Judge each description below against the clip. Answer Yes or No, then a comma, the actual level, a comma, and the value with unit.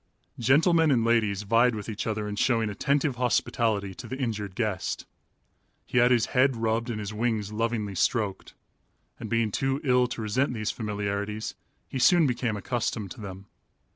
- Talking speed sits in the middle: Yes, average, 170 wpm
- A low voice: Yes, low, 115 Hz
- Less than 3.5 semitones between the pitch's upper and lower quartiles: Yes, average, 3.1 semitones